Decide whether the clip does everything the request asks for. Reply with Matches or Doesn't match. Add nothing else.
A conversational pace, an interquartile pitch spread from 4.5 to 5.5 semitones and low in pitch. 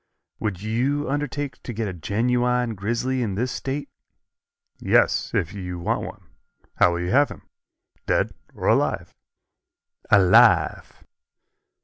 Doesn't match